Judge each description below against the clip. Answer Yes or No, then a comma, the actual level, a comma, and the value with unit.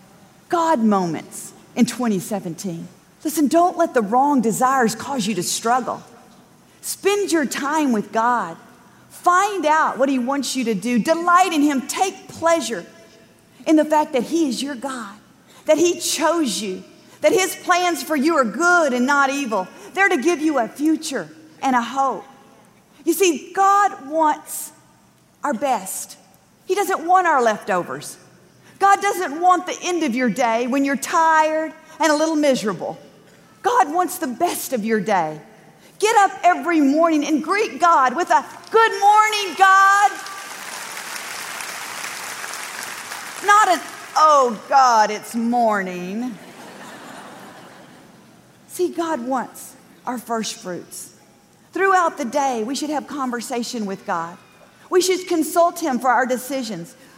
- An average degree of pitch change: No, wide, 6.6 semitones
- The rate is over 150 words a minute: No, average, 145 wpm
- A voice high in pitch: Yes, very high, 285 Hz